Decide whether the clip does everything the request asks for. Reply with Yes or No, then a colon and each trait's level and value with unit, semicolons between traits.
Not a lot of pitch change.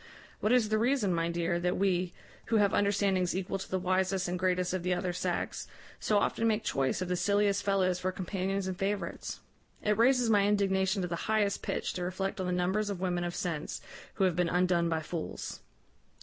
Yes: narrow, 2.2 semitones